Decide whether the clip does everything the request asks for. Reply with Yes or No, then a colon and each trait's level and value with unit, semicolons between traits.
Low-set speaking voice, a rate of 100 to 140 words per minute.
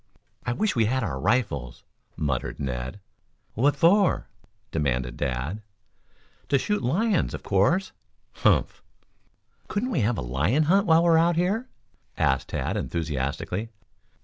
Yes: low, 115 Hz; slow, 135 wpm